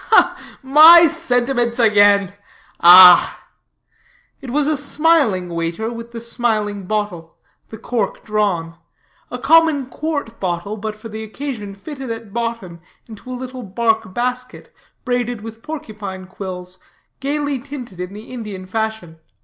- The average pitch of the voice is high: Yes, high, 225 Hz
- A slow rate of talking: Yes, slow, 130 wpm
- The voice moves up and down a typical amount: Yes, average, 4.3 semitones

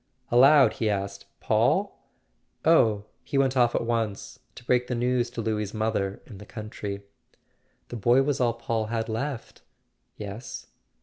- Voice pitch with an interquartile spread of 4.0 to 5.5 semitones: No, average, 2.8 semitones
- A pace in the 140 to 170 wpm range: Yes, average, 150 wpm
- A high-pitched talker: No, low, 115 Hz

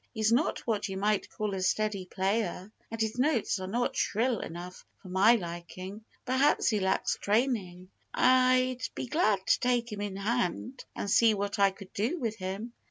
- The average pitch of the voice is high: Yes, high, 215 Hz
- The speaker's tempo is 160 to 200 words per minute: Yes, average, 180 wpm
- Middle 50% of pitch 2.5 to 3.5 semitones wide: No, average, 4.0 semitones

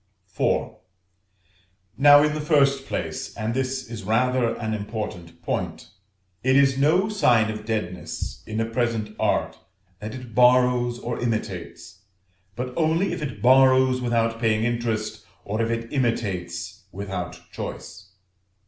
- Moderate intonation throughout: Yes, average, 3.3 semitones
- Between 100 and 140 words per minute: Yes, slow, 135 wpm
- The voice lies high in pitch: No, low, 115 Hz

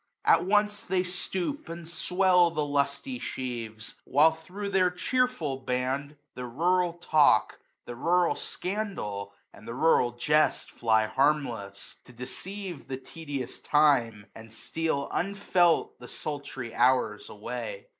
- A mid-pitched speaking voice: Yes, medium, 150 Hz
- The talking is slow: Yes, slow, 130 wpm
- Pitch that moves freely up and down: Yes, wide, 6.3 semitones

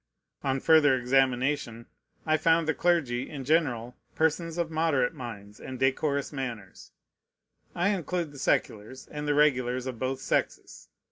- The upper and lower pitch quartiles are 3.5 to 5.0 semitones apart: Yes, average, 4.2 semitones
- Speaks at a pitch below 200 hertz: Yes, low, 135 Hz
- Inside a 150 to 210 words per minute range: No, average, 140 wpm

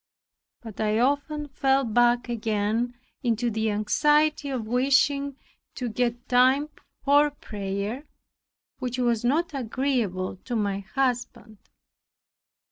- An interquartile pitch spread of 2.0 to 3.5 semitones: No, average, 3.9 semitones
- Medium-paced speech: No, slow, 110 wpm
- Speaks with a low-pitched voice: No, high, 245 Hz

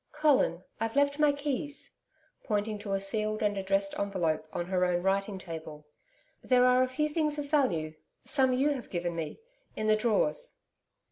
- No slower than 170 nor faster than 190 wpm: Yes, average, 175 wpm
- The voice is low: No, high, 215 Hz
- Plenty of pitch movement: Yes, wide, 6.9 semitones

